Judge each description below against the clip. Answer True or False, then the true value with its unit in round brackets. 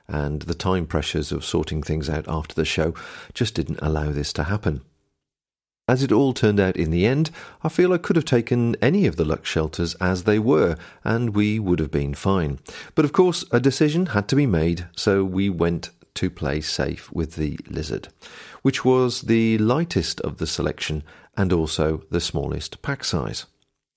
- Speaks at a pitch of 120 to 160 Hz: False (95 Hz)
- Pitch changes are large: True (7.4 semitones)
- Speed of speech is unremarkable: True (190 wpm)